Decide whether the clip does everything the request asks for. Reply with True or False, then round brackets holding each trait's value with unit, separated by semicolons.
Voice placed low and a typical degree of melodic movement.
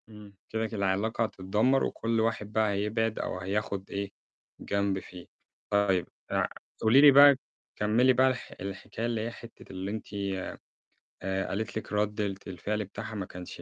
False (105 Hz; 2.3 semitones)